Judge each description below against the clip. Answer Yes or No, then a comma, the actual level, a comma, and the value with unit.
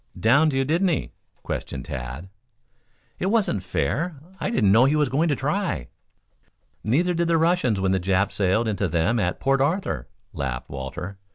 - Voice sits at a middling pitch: No, low, 120 Hz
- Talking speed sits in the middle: Yes, average, 170 wpm